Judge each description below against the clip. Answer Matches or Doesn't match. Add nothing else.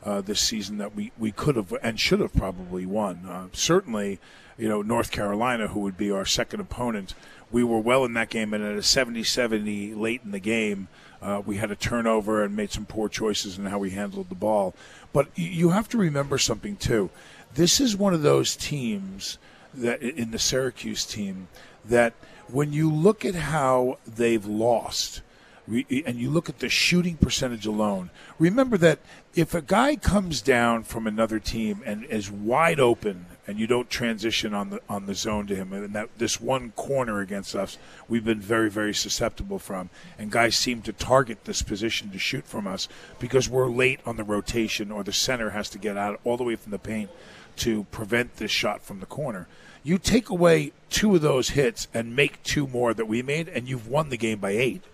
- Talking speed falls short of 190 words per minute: Doesn't match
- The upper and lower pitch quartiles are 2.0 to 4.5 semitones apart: Matches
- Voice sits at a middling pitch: Doesn't match